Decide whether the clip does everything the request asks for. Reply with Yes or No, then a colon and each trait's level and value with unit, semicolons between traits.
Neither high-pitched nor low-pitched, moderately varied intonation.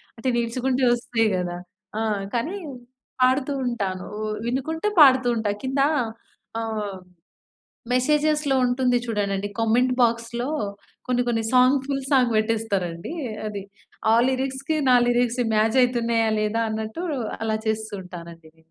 No: high, 235 Hz; average, 3.0 semitones